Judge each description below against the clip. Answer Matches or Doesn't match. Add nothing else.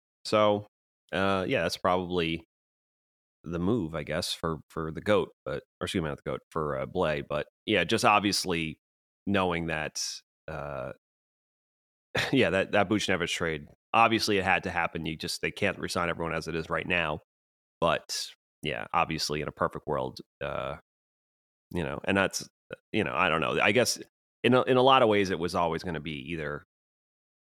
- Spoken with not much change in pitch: Doesn't match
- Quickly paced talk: Doesn't match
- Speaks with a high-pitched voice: Doesn't match